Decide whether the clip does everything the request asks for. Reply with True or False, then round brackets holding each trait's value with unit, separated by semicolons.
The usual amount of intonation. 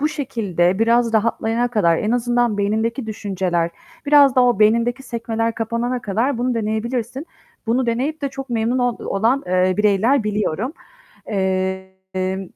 True (3.8 semitones)